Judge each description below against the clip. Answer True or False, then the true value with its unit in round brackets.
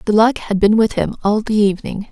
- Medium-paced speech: False (255 wpm)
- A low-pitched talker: False (210 Hz)